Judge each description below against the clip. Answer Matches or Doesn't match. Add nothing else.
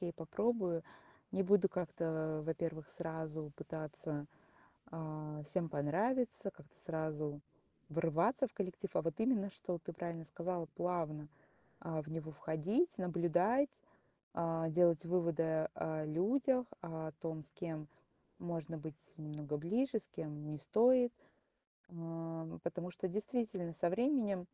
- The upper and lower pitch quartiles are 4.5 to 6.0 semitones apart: Doesn't match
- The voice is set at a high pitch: Doesn't match